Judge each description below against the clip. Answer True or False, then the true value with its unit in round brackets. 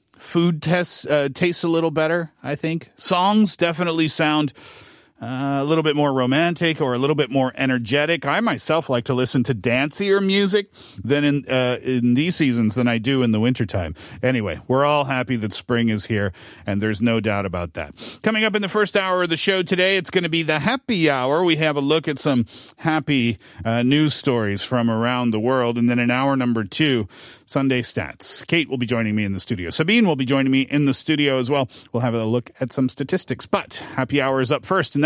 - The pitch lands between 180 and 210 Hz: False (135 Hz)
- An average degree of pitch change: True (5.0 semitones)